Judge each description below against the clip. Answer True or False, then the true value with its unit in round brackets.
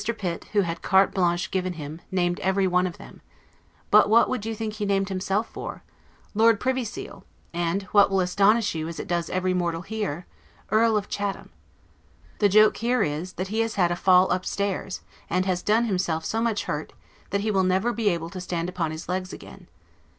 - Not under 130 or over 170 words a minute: False (200 wpm)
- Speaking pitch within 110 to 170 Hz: False (190 Hz)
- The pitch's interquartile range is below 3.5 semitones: True (2.9 semitones)